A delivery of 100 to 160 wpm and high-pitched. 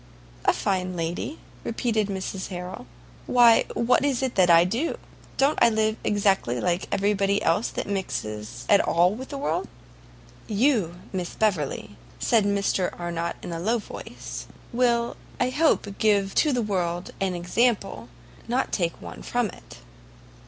Yes: average, 150 wpm; high, 200 Hz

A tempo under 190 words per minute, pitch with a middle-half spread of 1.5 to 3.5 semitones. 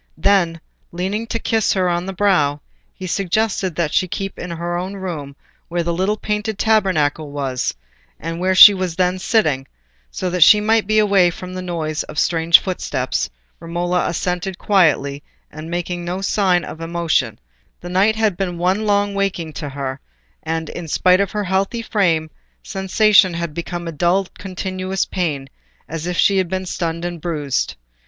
Yes: average, 175 wpm; average, 2.7 semitones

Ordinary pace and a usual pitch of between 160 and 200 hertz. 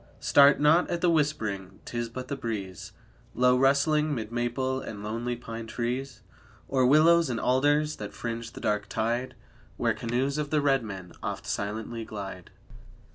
No: average, 160 wpm; low, 120 Hz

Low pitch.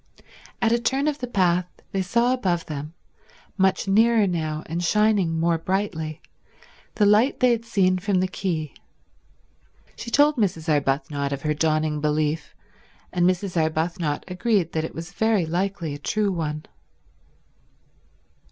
No: medium, 180 Hz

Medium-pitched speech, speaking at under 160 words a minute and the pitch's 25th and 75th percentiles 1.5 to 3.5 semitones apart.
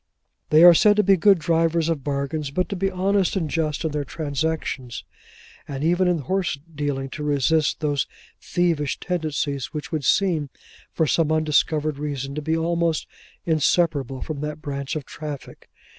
No: medium, 155 Hz; average, 165 wpm; average, 2.8 semitones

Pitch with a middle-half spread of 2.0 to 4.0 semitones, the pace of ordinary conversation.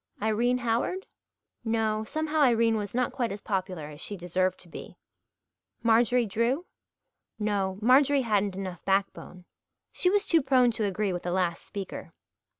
No: average, 4.5 semitones; average, 150 wpm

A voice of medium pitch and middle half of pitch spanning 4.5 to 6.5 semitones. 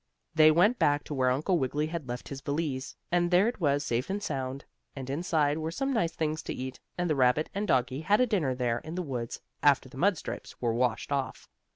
Yes: medium, 145 Hz; average, 4.8 semitones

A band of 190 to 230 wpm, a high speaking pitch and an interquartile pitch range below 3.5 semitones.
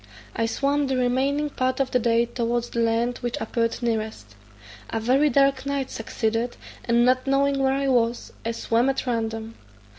No: average, 175 wpm; high, 245 Hz; average, 2.8 semitones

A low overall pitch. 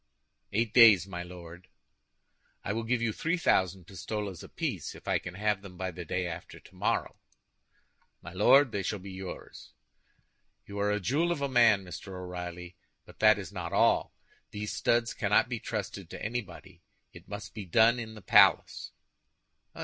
Yes: low, 100 Hz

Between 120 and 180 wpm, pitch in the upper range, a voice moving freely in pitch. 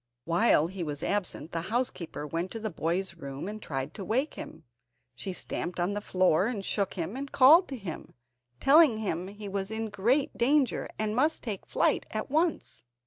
No: average, 195 wpm; high, 200 Hz; wide, 5.8 semitones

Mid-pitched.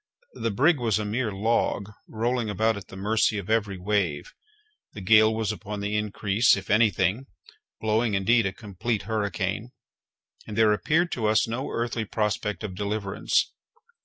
No: low, 105 Hz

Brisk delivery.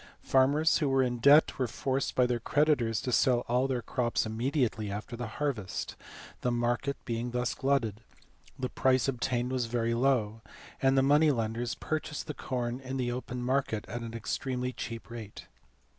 No: average, 170 wpm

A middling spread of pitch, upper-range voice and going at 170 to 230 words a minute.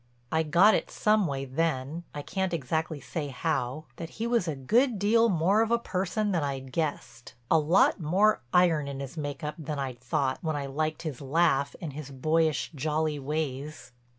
No: average, 3.8 semitones; medium, 155 Hz; average, 180 wpm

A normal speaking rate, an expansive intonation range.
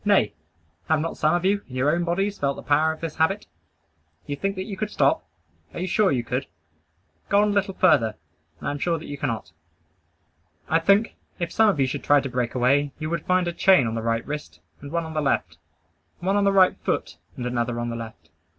No: fast, 235 wpm; wide, 6.5 semitones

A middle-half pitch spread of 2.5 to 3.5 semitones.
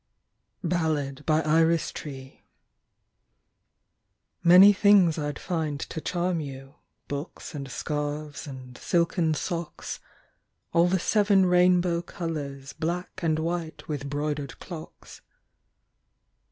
Yes: average, 3.2 semitones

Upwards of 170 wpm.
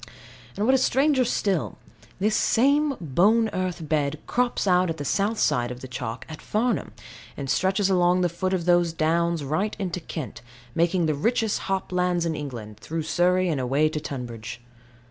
Yes: average, 180 wpm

